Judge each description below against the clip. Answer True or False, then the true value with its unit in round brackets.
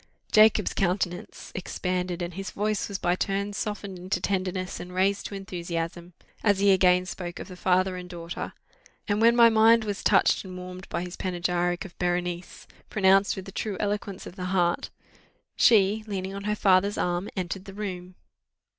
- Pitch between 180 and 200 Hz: True (185 Hz)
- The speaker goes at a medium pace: True (175 wpm)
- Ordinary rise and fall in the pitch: False (2.0 semitones)